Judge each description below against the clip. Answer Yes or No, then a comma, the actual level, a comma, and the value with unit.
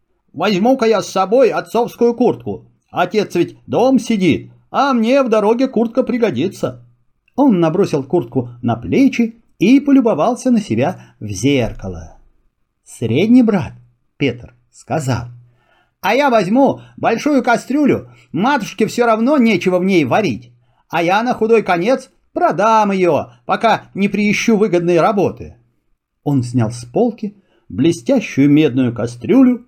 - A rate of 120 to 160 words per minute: Yes, average, 125 wpm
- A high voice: Yes, high, 195 Hz